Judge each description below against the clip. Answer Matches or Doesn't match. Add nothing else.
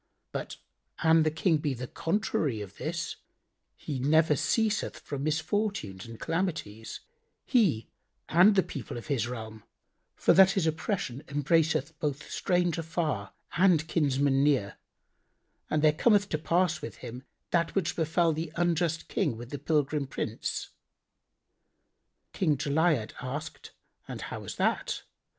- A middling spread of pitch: Matches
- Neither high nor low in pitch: Matches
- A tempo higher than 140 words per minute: Doesn't match